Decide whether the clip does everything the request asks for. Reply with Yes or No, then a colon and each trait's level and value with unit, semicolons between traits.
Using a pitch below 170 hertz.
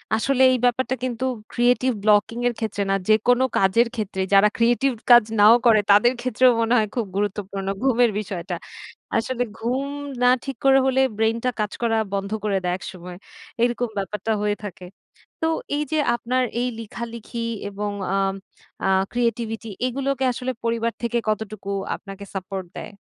No: high, 230 Hz